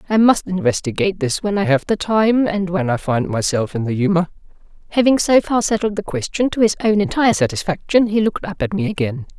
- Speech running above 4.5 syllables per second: Yes, 5.9 syllables/s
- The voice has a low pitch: No, medium, 185 Hz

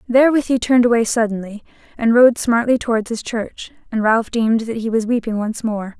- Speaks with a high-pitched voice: Yes, high, 230 Hz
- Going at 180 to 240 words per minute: Yes, average, 200 wpm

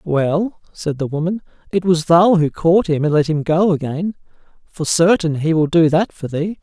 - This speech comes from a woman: No, male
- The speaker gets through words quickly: Yes, fast, 210 wpm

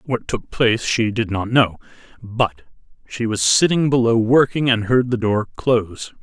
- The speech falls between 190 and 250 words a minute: No, average, 175 wpm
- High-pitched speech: No, low, 115 Hz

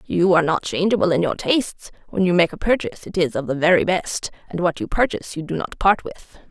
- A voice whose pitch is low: No, medium, 185 Hz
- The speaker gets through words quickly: Yes, fast, 250 wpm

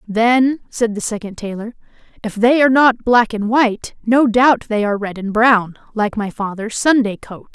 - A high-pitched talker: Yes, high, 225 Hz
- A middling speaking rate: Yes, average, 190 wpm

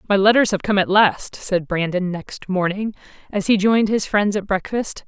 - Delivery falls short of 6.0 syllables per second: Yes, 4.9 syllables/s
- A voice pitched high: Yes, high, 200 Hz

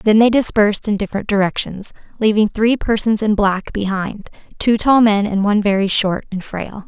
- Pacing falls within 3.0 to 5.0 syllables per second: No, 5.2 syllables/s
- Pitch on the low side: No, high, 205 Hz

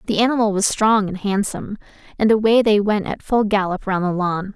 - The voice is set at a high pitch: Yes, high, 205 Hz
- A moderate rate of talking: No, fast, 210 wpm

